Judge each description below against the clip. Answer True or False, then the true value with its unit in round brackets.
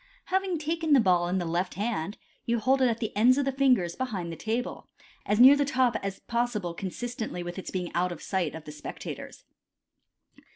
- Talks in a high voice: True (220 Hz)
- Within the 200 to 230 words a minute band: True (205 wpm)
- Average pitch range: False (6.5 semitones)